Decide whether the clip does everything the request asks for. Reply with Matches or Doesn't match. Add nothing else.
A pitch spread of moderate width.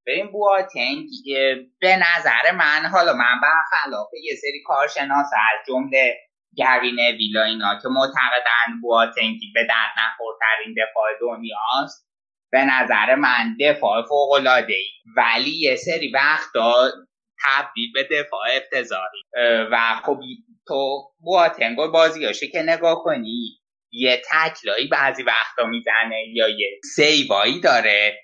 Doesn't match